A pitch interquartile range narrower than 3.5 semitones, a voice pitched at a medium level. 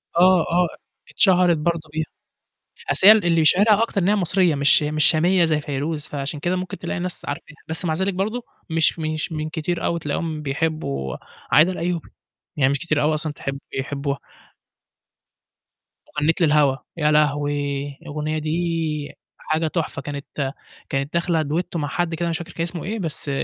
Yes: average, 2.8 semitones; medium, 160 Hz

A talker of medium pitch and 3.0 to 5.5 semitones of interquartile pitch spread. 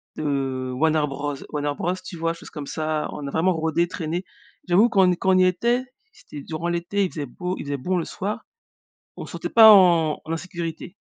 Yes: medium, 165 Hz; average, 3.5 semitones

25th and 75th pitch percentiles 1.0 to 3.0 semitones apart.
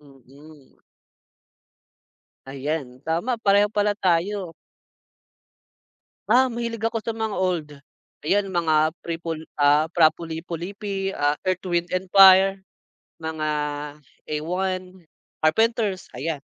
No: average, 4.3 semitones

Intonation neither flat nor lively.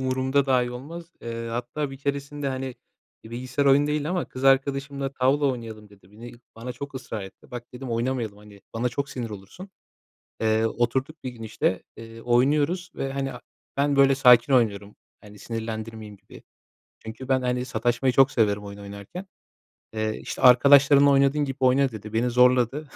Yes: average, 3.4 semitones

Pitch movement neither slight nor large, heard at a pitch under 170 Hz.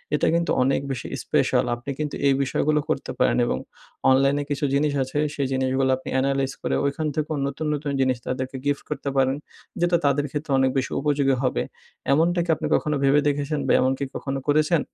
No: narrow, 2.0 semitones; medium, 140 Hz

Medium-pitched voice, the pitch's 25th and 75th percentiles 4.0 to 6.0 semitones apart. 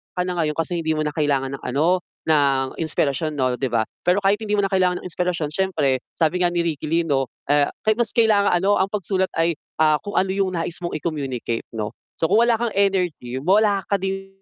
Yes: medium, 170 Hz; average, 4.7 semitones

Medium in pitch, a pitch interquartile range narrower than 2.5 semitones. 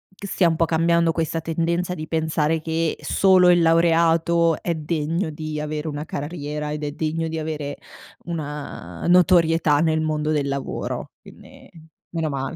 Yes: medium, 160 Hz; narrow, 1.8 semitones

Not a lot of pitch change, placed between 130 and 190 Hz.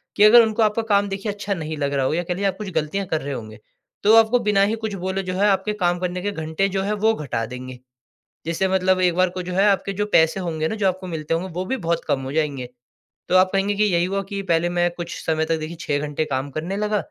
No: average, 4.0 semitones; medium, 185 Hz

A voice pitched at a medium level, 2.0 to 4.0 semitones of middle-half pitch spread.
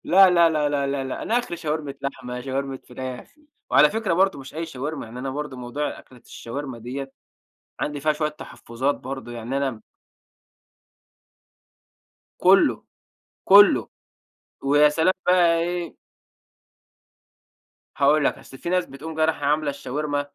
Yes: medium, 145 Hz; average, 3.3 semitones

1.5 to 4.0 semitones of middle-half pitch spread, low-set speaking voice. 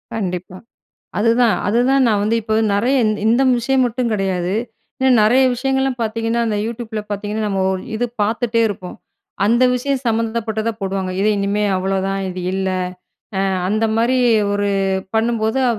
No: average, 2.8 semitones; high, 220 Hz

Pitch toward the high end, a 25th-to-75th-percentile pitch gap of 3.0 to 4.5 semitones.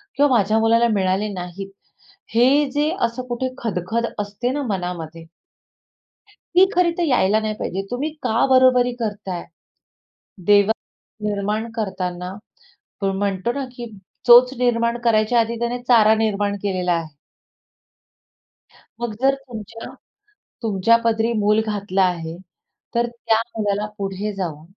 Yes: high, 220 Hz; average, 3.4 semitones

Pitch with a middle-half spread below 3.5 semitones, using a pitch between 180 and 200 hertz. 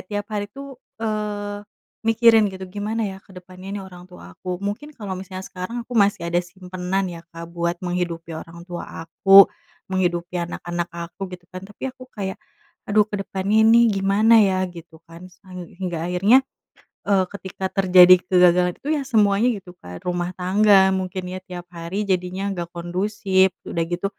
Yes: narrow, 2.5 semitones; medium, 185 Hz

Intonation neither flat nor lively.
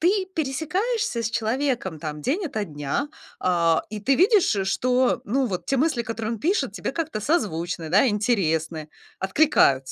No: wide, 8.5 semitones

